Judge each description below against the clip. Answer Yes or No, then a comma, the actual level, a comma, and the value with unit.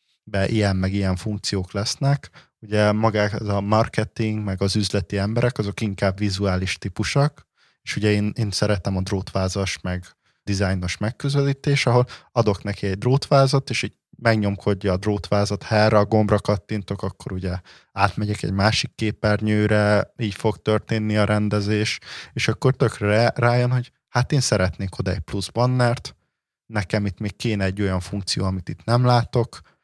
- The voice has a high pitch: No, low, 105 Hz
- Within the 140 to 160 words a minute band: Yes, fast, 155 wpm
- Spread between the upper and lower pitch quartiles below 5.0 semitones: Yes, narrow, 2.4 semitones